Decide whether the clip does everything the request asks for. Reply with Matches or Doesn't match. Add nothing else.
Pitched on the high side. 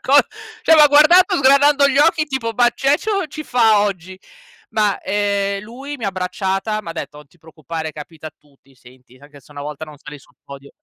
Matches